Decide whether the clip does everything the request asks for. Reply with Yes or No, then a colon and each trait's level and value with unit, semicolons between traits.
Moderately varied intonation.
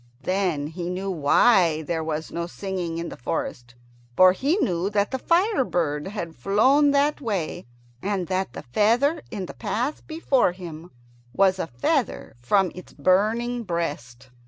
No: wide, 6.0 semitones